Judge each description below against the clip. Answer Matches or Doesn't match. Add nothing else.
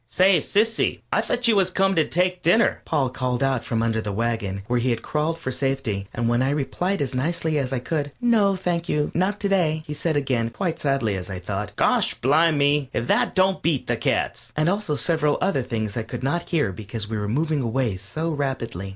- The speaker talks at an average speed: Doesn't match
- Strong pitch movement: Matches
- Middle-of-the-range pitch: Matches